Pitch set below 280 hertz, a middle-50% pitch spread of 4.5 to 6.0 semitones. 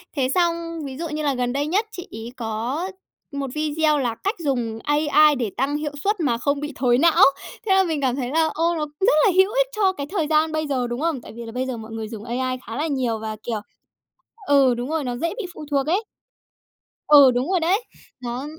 No: very high, 285 Hz; average, 4.8 semitones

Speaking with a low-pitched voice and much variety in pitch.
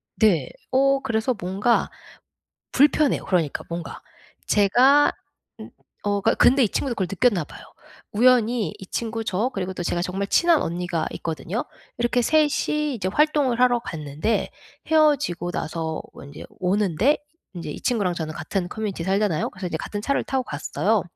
No: high, 205 Hz; wide, 6.2 semitones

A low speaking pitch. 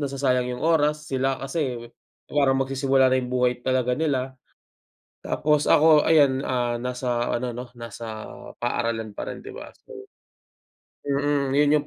Yes: low, 130 Hz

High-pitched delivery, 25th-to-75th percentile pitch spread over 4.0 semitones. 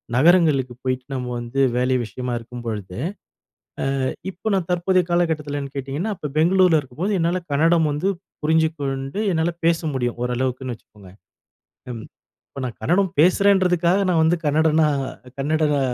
No: medium, 155 Hz; average, 5.1 semitones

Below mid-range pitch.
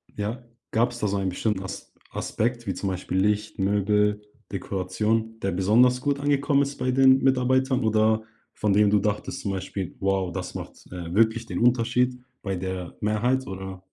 Yes: low, 105 Hz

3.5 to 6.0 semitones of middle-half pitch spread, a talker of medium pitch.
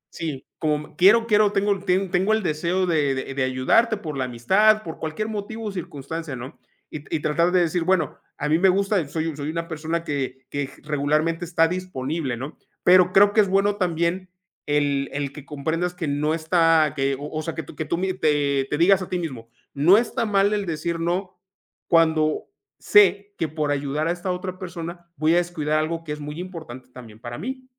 Yes: average, 3.9 semitones; medium, 165 Hz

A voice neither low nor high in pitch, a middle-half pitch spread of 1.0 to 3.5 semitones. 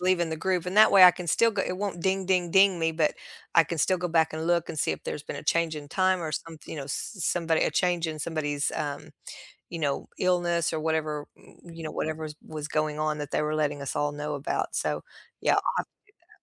Yes: medium, 160 Hz; average, 2.8 semitones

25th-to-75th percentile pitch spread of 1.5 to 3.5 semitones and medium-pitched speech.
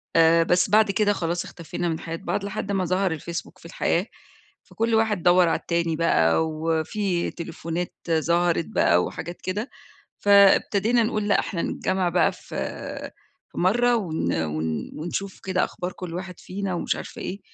Yes: average, 3.1 semitones; medium, 175 Hz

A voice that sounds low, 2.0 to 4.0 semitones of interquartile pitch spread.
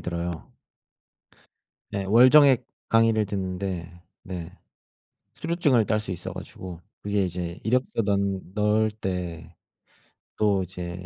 Yes: very low, 95 Hz; average, 3.2 semitones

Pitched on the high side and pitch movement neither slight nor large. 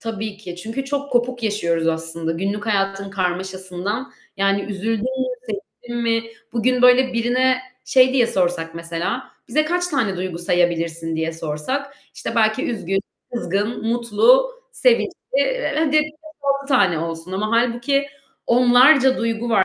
No: high, 225 Hz; wide, 5.7 semitones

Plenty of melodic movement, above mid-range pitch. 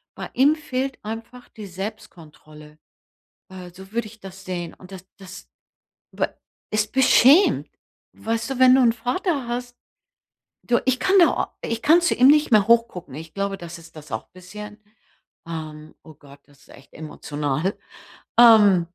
Yes: wide, 6.6 semitones; high, 210 Hz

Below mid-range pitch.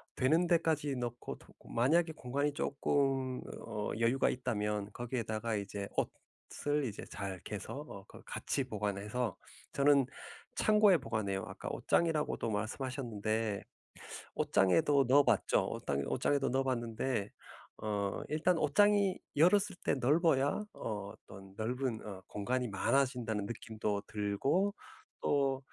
Yes: low, 125 Hz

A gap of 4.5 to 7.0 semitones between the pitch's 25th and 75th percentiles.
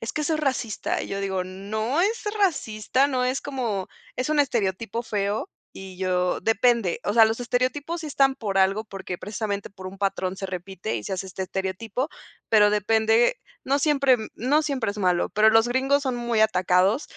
Yes: average, 4.9 semitones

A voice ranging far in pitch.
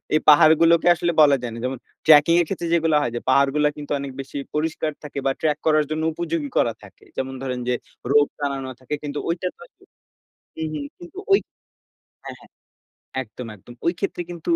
No: average, 3.2 semitones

